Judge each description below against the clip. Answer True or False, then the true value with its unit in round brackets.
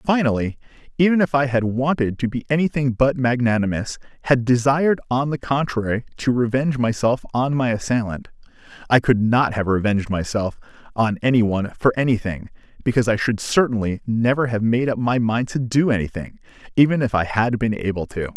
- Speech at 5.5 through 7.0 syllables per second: True (5.6 syllables/s)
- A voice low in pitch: True (120 Hz)